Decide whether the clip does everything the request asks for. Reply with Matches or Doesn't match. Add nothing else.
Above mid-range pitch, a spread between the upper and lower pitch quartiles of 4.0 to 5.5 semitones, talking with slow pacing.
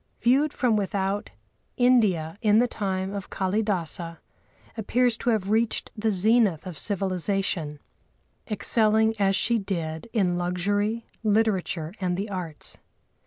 Doesn't match